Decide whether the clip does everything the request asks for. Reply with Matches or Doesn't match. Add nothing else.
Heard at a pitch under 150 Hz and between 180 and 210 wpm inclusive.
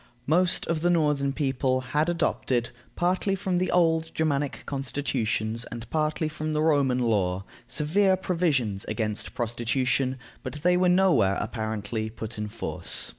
Doesn't match